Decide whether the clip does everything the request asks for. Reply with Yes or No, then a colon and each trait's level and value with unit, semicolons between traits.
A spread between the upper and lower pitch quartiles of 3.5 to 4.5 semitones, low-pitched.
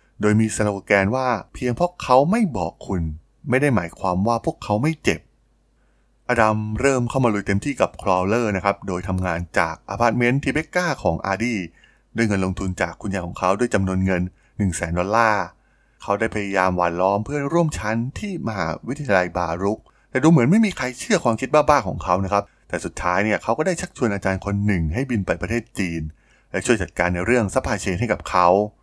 No: average, 4.9 semitones; low, 105 Hz